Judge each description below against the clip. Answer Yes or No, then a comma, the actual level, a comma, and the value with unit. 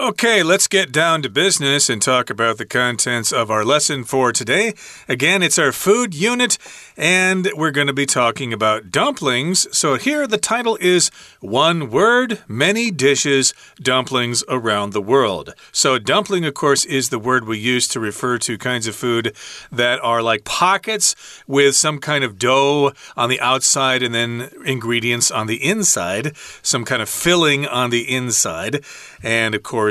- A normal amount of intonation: No, wide, 6.3 semitones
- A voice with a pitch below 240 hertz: Yes, low, 135 Hz